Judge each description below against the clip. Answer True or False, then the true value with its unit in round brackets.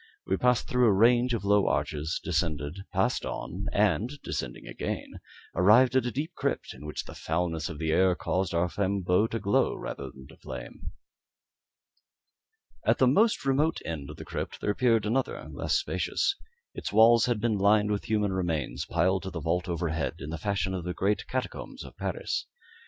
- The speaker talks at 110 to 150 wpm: False (180 wpm)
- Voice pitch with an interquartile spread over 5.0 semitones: True (5.4 semitones)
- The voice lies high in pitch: False (100 Hz)